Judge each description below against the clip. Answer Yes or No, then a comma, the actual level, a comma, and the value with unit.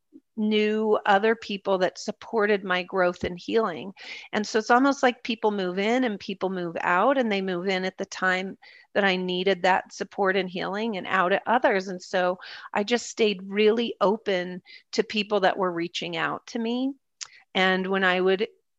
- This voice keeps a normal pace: Yes, average, 185 wpm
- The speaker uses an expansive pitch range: No, average, 3.2 semitones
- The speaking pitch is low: No, high, 200 Hz